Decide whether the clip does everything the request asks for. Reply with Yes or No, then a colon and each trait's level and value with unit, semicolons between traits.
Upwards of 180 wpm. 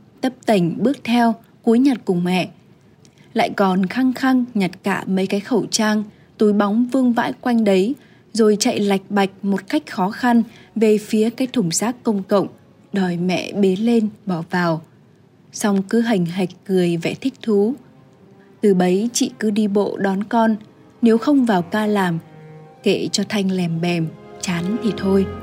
No: average, 175 wpm